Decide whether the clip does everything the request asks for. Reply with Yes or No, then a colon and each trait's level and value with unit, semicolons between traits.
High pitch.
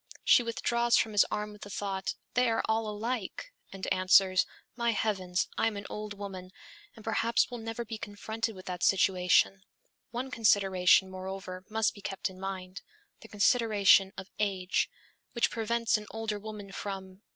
Yes: high, 205 Hz